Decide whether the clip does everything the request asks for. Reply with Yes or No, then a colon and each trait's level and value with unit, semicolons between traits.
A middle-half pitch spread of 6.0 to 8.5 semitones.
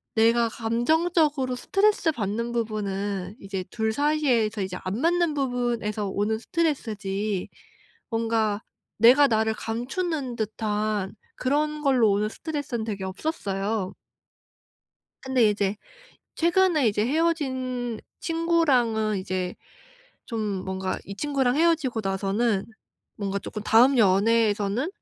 No: wide, 5.4 semitones